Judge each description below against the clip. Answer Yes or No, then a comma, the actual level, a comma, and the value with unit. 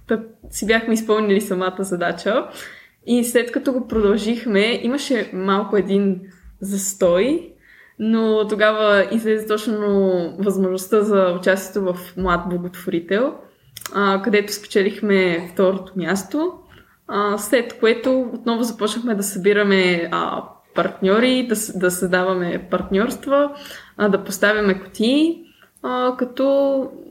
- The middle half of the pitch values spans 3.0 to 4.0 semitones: Yes, average, 3.6 semitones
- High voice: Yes, high, 205 Hz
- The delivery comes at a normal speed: No, slow, 95 wpm